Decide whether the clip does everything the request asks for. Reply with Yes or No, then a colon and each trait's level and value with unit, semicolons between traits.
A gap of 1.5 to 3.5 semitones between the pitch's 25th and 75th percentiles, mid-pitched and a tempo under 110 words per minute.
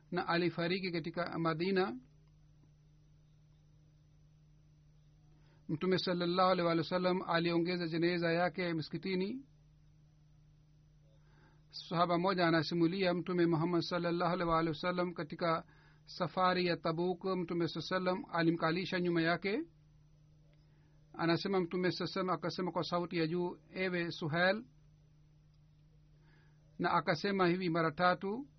Yes: average, 2.9 semitones; medium, 170 Hz; slow, 100 wpm